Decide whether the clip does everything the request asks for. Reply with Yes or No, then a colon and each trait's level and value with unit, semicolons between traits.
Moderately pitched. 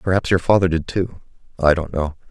No: very low, 85 Hz